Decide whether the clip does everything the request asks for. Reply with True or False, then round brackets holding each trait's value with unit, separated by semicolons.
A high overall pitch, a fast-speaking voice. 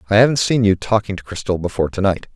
False (105 Hz; 255 wpm)